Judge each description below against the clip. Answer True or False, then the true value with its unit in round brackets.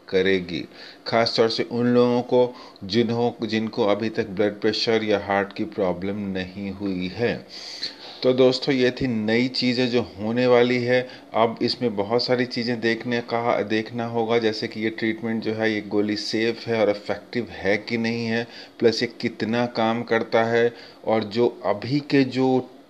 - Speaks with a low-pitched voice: True (115 Hz)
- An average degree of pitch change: False (1.9 semitones)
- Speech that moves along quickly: False (170 wpm)